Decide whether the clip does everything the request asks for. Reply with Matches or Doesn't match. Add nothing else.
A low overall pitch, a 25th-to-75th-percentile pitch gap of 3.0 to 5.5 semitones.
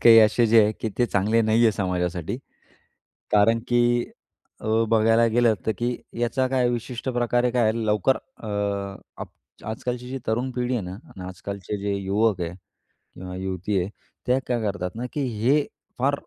Matches